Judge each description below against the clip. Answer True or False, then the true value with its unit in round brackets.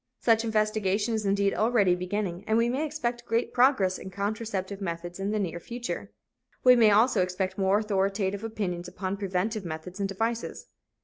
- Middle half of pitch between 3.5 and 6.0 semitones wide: False (3.1 semitones)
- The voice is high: True (200 Hz)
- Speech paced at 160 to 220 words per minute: True (170 wpm)